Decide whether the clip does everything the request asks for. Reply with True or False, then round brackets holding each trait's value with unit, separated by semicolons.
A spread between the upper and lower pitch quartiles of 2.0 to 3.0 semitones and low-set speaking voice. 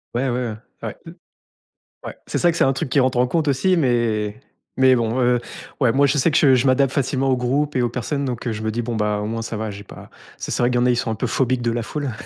True (2.7 semitones; 125 Hz)